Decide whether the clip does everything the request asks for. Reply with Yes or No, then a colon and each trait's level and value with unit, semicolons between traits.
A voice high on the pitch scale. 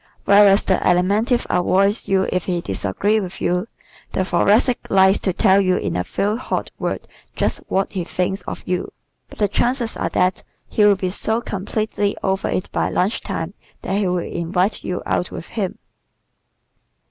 Yes: high, 195 Hz